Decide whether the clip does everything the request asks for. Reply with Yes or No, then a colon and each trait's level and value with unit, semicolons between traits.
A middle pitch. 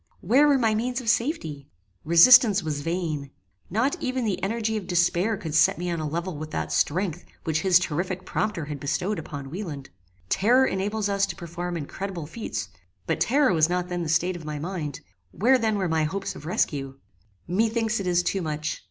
Yes: medium, 180 Hz